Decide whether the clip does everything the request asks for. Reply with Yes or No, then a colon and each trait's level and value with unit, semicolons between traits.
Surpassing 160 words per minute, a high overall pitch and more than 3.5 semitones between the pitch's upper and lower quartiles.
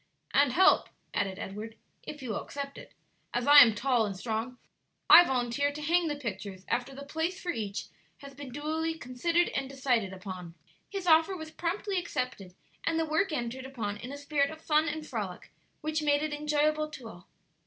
Yes: average, 190 wpm; very high, 280 Hz; average, 5.1 semitones